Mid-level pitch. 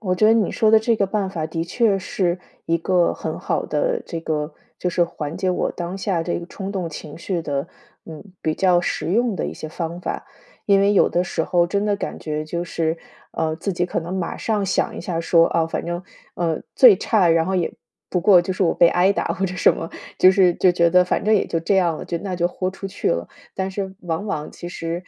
Yes: medium, 180 Hz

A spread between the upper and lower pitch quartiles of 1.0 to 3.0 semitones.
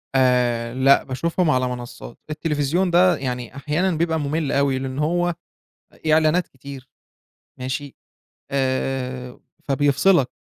No: average, 3.6 semitones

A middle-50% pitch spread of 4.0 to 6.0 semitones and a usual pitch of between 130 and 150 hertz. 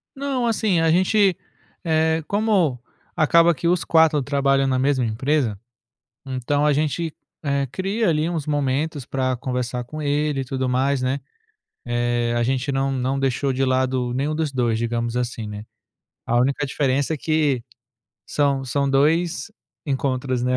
No: average, 3.5 semitones; medium, 140 Hz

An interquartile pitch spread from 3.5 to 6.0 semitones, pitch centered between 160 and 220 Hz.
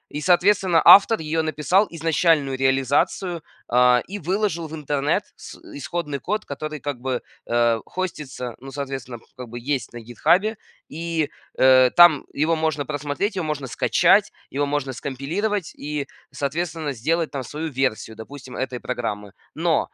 No: average, 4.1 semitones; medium, 145 Hz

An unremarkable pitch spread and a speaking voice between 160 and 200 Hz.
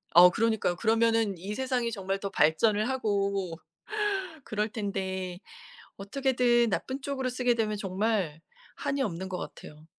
No: average, 4.0 semitones; high, 210 Hz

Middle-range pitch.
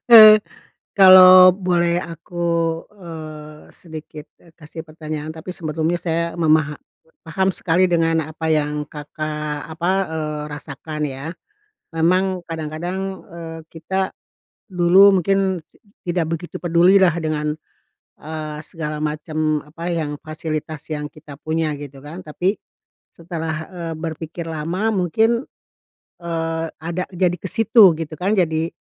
Yes: medium, 165 Hz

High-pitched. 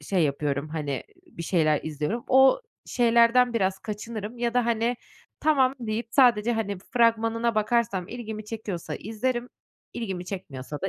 Yes: high, 225 Hz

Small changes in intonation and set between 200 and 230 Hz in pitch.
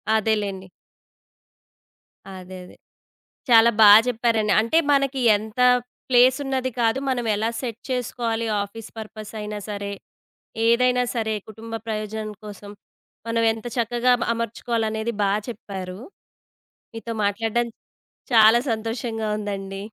Yes: narrow, 2.1 semitones; high, 225 Hz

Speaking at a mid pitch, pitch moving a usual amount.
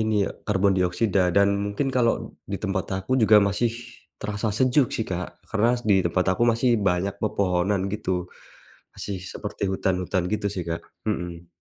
No: low, 100 Hz; average, 3.0 semitones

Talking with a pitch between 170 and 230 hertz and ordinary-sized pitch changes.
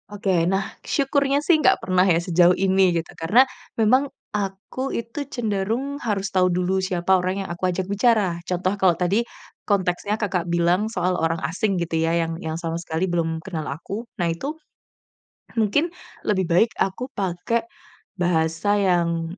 Yes: medium, 185 Hz; average, 3.4 semitones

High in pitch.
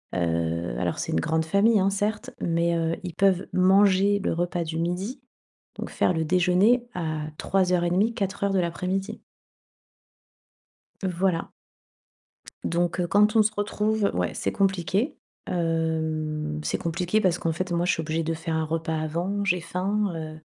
No: medium, 175 Hz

